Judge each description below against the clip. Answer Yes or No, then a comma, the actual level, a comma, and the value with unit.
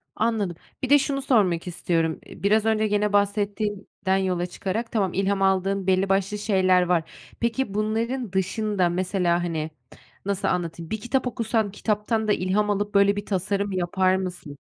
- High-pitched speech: Yes, high, 200 Hz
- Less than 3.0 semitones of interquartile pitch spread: Yes, narrow, 2.5 semitones